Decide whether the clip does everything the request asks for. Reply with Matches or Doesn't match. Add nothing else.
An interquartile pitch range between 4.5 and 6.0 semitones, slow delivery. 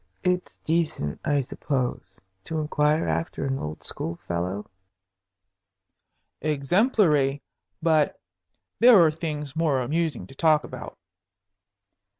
Doesn't match